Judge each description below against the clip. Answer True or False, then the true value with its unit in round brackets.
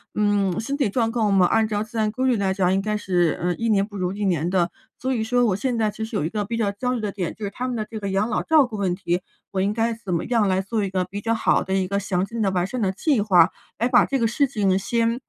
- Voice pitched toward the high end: True (210 Hz)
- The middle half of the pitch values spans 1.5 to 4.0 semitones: True (3.2 semitones)